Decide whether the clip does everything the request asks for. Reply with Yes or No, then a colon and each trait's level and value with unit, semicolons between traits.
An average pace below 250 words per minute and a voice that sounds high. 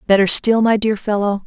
Yes: fast, 205 wpm; high, 210 Hz